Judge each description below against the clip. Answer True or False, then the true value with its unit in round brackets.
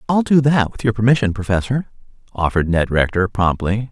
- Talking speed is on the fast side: False (170 wpm)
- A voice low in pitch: True (110 Hz)